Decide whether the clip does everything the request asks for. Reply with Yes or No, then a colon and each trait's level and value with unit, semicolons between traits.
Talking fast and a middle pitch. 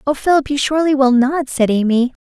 No: fast, 215 wpm; very high, 270 Hz